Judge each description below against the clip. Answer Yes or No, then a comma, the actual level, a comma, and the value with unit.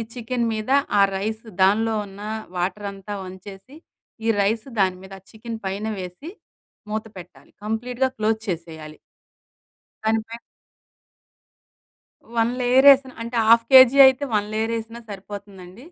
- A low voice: No, high, 220 Hz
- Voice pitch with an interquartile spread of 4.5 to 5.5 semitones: No, average, 3.2 semitones